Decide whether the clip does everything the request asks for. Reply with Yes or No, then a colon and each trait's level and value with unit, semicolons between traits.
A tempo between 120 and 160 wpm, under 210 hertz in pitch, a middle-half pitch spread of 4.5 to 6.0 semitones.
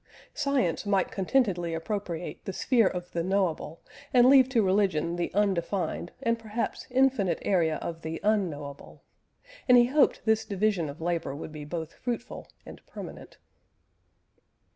Yes: average, 140 wpm; high, 190 Hz; average, 5.3 semitones